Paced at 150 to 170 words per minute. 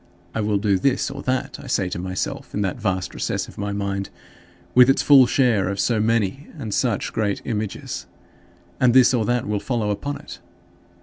No: average, 195 wpm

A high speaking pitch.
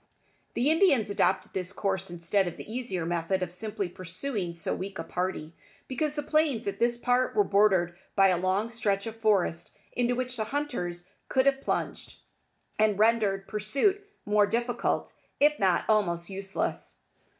Yes: high, 205 Hz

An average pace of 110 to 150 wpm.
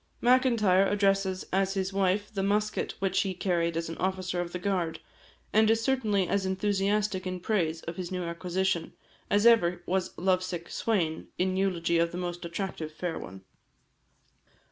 No: average, 165 wpm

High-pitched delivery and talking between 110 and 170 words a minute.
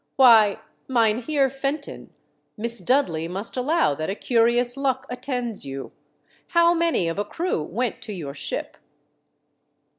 Yes: high, 240 Hz; average, 140 wpm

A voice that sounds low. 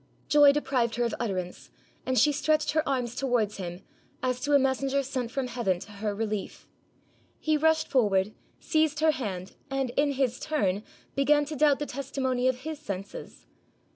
No: very high, 260 Hz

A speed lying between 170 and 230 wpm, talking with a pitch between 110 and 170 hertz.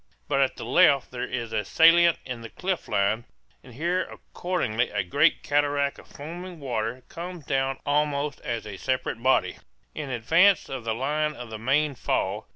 Yes: average, 175 wpm; low, 135 Hz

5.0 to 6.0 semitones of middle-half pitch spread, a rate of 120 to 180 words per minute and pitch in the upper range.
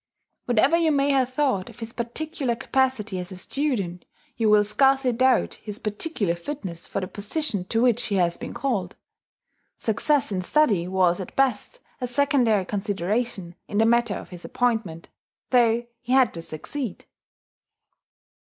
Yes: wide, 5.5 semitones; average, 155 wpm; high, 230 Hz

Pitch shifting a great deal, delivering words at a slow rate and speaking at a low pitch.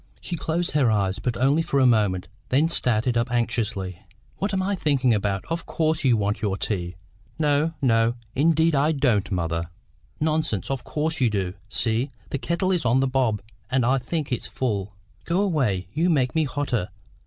No: wide, 6.6 semitones; average, 185 wpm; low, 130 Hz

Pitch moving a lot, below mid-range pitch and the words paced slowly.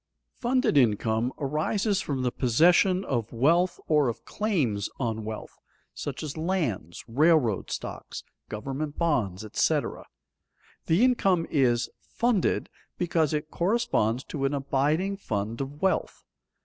No: wide, 6.9 semitones; medium, 145 Hz; slow, 125 wpm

